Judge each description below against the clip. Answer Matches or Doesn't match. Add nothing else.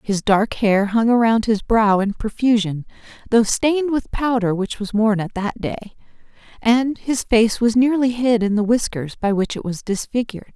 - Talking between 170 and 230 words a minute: Matches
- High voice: Matches